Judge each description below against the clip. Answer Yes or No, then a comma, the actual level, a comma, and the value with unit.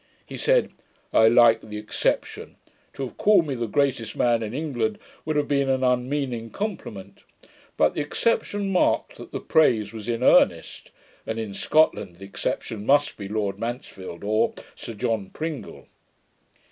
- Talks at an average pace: Yes, average, 160 wpm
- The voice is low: Yes, low, 120 Hz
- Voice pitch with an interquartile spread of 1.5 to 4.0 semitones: No, average, 5.2 semitones